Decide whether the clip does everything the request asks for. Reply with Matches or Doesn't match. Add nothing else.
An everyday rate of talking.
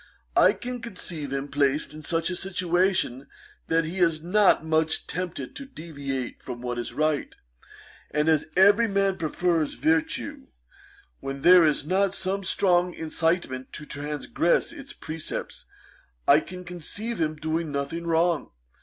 Matches